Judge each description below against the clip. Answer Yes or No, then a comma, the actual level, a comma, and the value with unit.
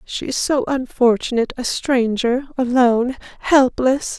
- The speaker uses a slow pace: Yes, slow, 115 wpm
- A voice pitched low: No, very high, 255 Hz